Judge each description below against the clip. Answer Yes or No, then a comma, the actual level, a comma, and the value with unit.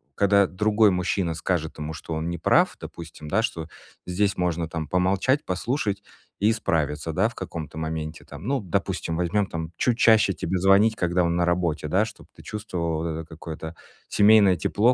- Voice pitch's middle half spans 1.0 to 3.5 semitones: No, average, 4.2 semitones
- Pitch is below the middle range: Yes, very low, 90 Hz